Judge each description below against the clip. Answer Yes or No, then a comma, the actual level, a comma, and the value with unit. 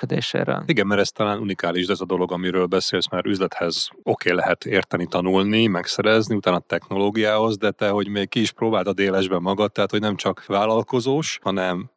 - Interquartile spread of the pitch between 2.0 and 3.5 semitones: Yes, narrow, 2.6 semitones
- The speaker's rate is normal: No, fast, 185 wpm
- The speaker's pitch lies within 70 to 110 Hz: Yes, low, 100 Hz